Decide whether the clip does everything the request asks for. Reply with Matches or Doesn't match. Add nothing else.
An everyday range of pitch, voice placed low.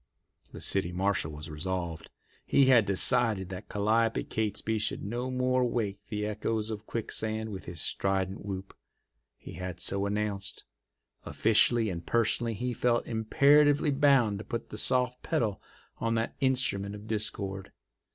Matches